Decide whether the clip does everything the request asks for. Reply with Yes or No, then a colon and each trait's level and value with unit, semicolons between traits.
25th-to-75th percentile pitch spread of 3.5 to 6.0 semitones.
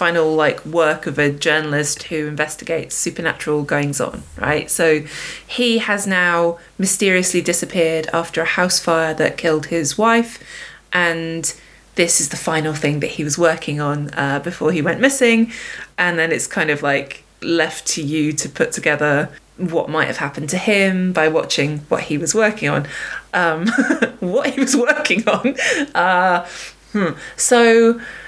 Yes: average, 3.9 semitones